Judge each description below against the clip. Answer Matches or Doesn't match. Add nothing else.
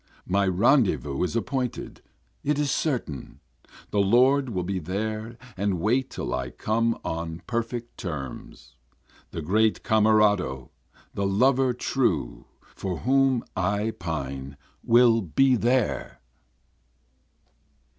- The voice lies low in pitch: Matches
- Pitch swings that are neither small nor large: Doesn't match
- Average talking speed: Doesn't match